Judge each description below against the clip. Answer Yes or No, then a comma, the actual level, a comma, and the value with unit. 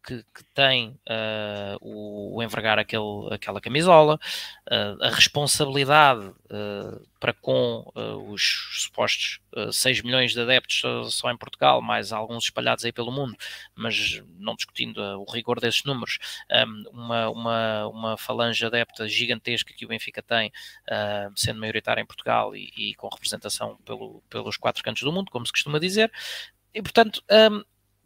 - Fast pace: No, average, 160 wpm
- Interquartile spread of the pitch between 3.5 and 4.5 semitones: Yes, average, 3.9 semitones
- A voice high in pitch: No, low, 115 Hz